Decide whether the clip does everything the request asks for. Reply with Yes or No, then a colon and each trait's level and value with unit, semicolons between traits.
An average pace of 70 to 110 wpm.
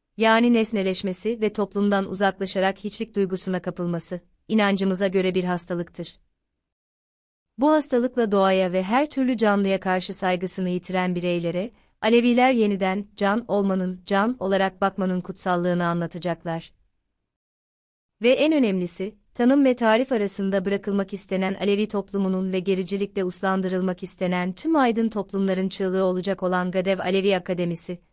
No: average, 120 wpm